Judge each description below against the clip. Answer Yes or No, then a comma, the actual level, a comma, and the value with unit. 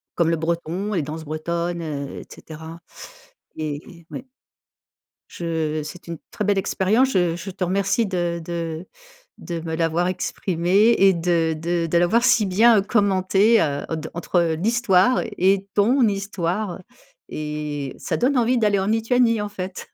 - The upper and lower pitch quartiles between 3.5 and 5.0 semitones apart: Yes, average, 3.8 semitones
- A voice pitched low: No, medium, 175 Hz